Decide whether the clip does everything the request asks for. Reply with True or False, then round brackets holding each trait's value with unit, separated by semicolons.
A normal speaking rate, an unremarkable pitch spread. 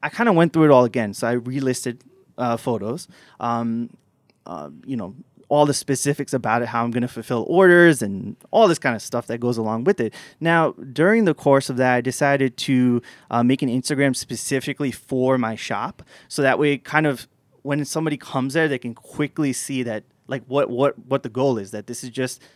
False (215 wpm; 3.0 semitones)